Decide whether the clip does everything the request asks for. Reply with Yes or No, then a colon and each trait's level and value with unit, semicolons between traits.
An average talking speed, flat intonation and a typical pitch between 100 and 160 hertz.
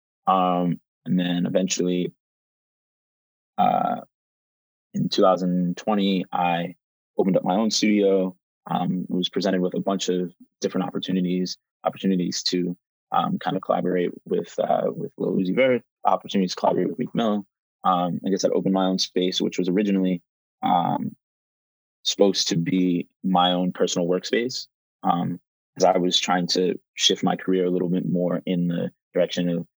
No: average, 150 wpm; narrow, 1.0 semitones; very low, 90 Hz